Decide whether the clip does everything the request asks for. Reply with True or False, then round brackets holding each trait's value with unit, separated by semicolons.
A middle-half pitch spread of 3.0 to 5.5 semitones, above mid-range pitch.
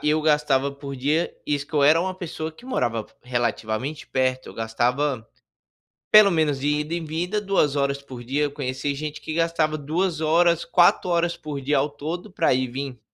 False (3.4 semitones; 150 Hz)